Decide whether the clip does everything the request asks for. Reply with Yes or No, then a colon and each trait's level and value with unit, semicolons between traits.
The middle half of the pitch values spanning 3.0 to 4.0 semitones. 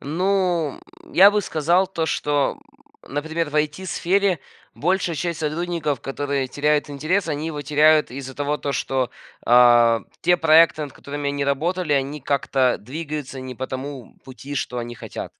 Yes: average, 3.5 semitones